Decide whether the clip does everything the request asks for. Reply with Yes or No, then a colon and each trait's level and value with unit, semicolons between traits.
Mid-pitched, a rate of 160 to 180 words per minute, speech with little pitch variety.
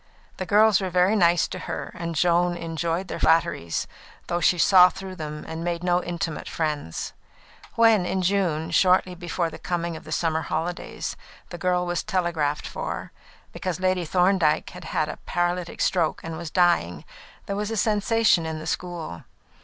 Yes: medium, 175 Hz; average, 170 wpm; narrow, 2.2 semitones